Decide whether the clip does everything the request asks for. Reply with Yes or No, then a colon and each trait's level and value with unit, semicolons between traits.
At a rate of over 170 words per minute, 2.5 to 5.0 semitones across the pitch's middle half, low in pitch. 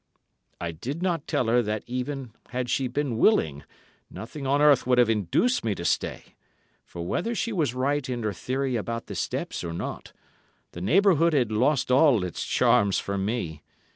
No: average, 180 wpm; wide, 5.4 semitones; low, 125 Hz